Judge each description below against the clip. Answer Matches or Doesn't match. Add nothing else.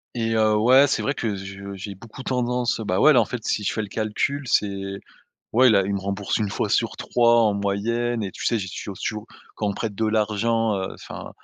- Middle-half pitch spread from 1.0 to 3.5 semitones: Matches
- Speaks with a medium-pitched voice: Doesn't match